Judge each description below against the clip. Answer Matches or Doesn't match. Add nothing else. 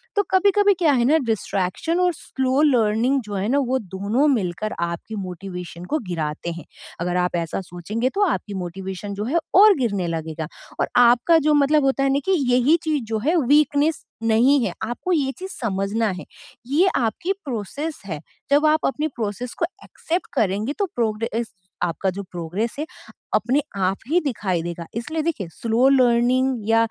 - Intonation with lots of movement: Matches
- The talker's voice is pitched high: Matches